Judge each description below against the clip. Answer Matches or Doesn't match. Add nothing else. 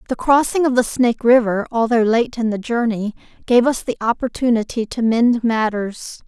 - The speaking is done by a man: Doesn't match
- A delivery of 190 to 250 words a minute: Doesn't match